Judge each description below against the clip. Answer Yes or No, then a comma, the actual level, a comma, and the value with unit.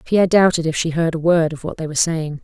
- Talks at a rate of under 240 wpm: No, fast, 295 wpm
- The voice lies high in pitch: No, medium, 165 Hz